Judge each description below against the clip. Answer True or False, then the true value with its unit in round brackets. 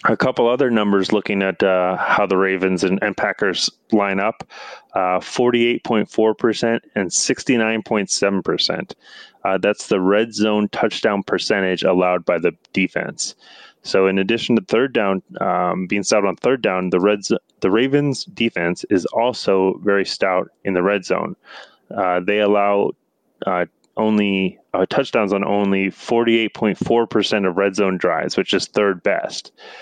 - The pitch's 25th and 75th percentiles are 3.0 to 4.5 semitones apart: False (2.6 semitones)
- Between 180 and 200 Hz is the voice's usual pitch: False (100 Hz)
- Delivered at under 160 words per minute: True (145 wpm)